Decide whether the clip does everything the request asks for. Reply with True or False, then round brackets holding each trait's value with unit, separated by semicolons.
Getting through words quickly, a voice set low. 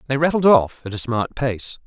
True (225 wpm; 130 Hz)